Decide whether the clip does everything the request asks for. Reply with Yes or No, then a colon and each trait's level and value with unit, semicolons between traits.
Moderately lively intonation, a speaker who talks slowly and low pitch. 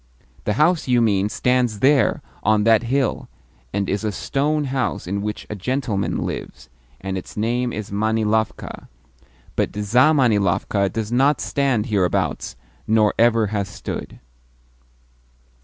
Yes: average, 3.6 semitones; slow, 130 wpm; low, 110 Hz